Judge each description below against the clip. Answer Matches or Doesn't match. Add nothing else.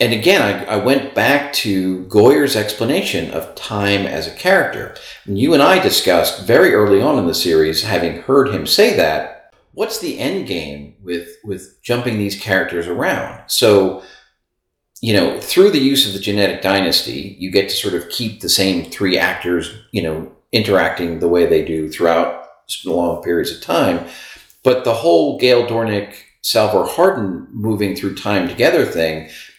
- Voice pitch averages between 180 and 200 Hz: Doesn't match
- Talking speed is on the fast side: Doesn't match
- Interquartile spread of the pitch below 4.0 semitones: Doesn't match